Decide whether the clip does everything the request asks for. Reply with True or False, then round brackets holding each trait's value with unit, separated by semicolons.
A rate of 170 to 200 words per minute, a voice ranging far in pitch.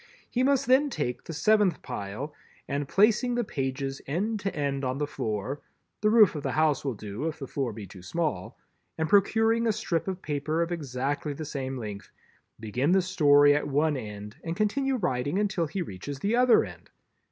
True (185 wpm; 7.1 semitones)